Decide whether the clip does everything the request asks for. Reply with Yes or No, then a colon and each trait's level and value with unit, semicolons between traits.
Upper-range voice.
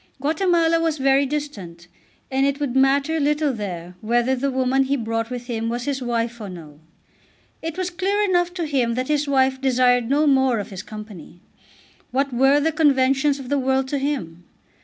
Yes: very high, 265 Hz